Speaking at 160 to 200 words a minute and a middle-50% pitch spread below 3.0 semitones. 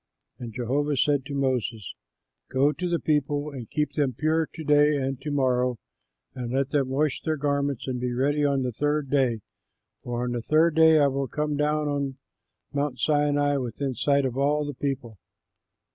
Yes: average, 185 wpm; narrow, 2.4 semitones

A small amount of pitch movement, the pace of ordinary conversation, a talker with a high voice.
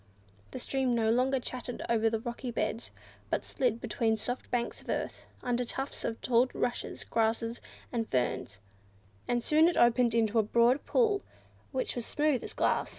Yes: narrow, 2.1 semitones; average, 165 wpm; high, 240 Hz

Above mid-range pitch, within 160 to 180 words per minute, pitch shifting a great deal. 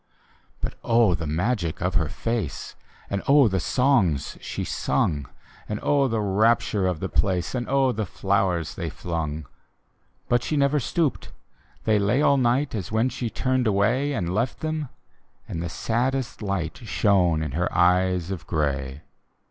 No: low, 105 Hz; average, 165 wpm; wide, 6.3 semitones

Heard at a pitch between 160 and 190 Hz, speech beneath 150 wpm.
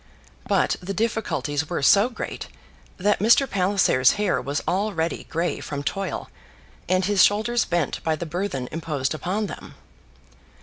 Yes: medium, 185 Hz; average, 140 wpm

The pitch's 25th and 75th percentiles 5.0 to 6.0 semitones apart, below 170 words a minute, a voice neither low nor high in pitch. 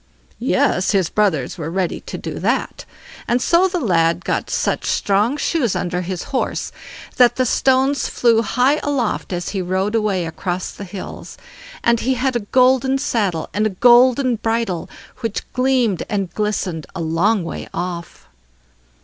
No: wide, 5.6 semitones; average, 160 wpm; high, 215 Hz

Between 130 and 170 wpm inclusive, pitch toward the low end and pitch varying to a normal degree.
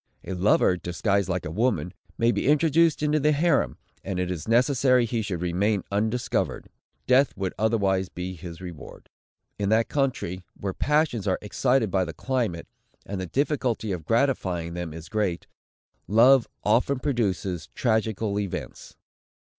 No: average, 155 wpm; low, 105 Hz; wide, 5.7 semitones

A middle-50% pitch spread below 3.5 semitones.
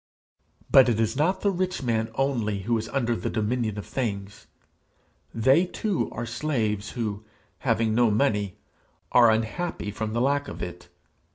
No: average, 4.1 semitones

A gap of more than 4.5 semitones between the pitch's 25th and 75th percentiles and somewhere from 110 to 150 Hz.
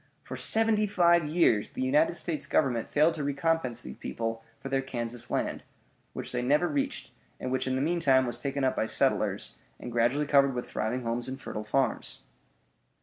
Yes: average, 5.1 semitones; low, 135 Hz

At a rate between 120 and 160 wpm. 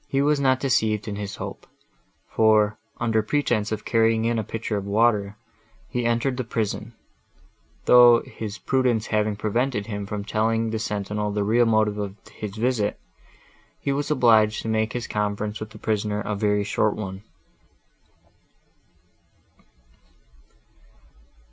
Yes: average, 140 wpm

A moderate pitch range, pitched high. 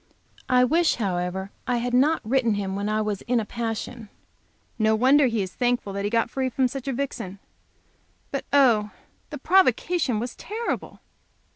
Yes: average, 4.0 semitones; high, 240 Hz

